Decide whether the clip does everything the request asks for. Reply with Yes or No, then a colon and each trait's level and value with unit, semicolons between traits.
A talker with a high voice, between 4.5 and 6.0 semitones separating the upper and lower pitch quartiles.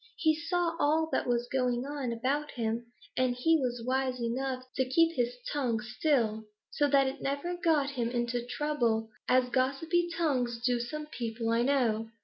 No: very high, 255 Hz; average, 3.6 semitones